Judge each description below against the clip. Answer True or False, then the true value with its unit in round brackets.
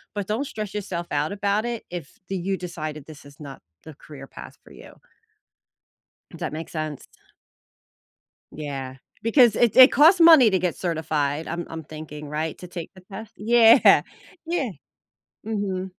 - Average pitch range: False (5.7 semitones)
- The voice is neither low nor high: True (180 Hz)